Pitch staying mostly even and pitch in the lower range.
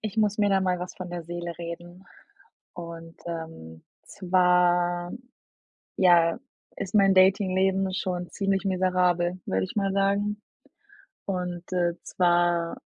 No: narrow, 1.8 semitones; medium, 180 Hz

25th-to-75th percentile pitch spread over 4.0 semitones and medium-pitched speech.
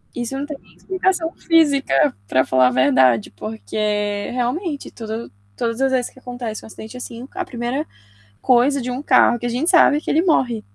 No: average, 5.1 semitones; high, 245 Hz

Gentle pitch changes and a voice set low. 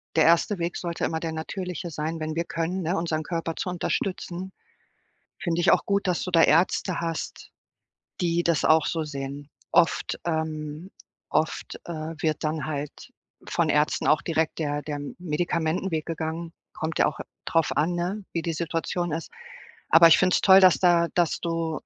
No: narrow, 1.7 semitones; medium, 165 Hz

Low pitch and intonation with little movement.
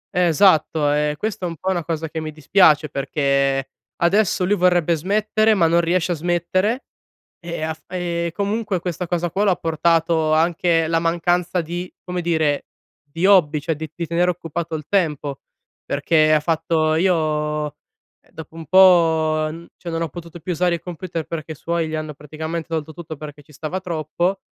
No: medium, 165 Hz; narrow, 2.3 semitones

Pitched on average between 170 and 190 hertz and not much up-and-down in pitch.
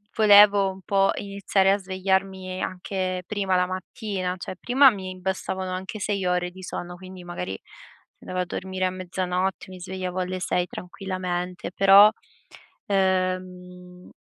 Yes: medium, 185 Hz; narrow, 1.2 semitones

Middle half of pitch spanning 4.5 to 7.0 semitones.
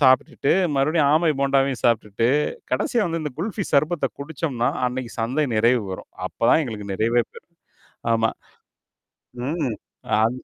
Yes: average, 4.9 semitones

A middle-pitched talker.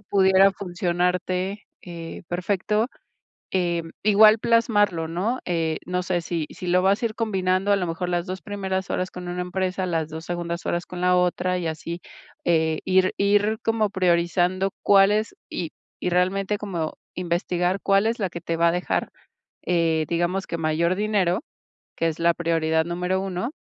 Yes: medium, 180 Hz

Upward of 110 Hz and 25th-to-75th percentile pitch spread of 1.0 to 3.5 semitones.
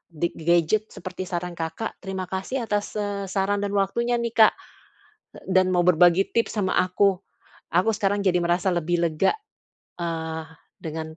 Yes: medium, 185 Hz; average, 2.8 semitones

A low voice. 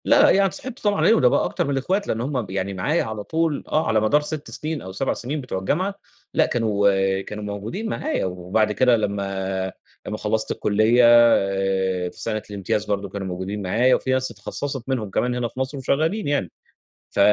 Yes: low, 110 Hz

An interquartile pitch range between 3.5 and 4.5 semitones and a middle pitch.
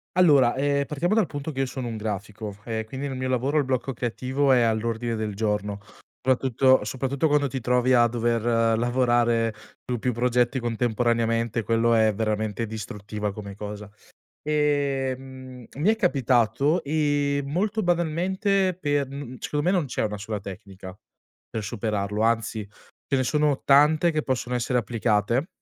No: average, 4.2 semitones; low, 125 Hz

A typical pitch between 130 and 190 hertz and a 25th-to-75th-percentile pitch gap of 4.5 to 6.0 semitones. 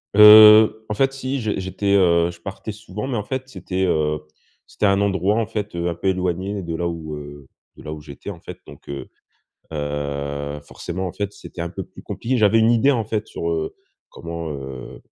No: very low, 95 Hz; average, 5.0 semitones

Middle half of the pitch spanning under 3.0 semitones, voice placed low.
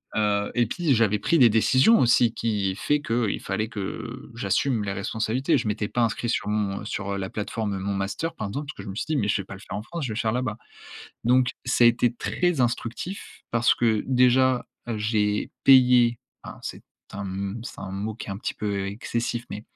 No: average, 3.3 semitones; low, 115 Hz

